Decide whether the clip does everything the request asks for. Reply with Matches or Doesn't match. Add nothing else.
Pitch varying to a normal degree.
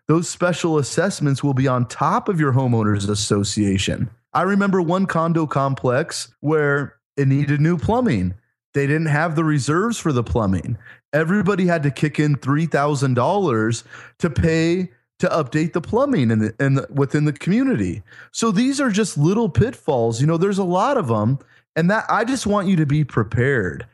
Doesn't match